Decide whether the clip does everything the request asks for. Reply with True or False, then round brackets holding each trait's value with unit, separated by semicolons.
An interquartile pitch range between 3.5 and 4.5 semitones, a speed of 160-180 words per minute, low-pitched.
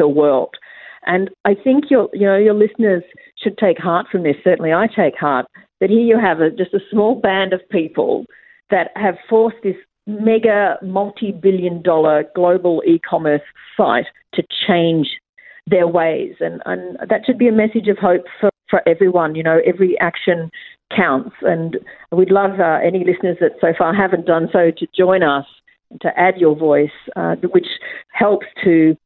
False (3.9 semitones; 170 wpm; 185 Hz)